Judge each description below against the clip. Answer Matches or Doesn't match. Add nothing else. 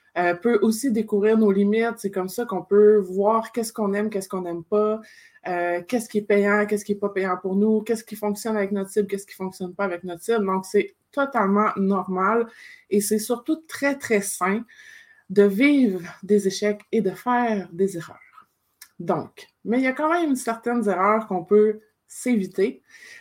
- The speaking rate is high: Doesn't match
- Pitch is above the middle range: Matches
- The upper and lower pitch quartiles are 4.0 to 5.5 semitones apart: Doesn't match